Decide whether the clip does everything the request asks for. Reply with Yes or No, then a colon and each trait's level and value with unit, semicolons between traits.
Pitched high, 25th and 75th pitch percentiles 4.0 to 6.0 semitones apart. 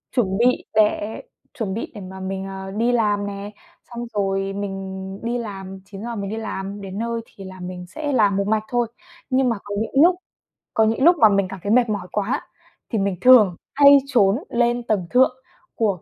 No: high, 205 Hz; average, 3.5 semitones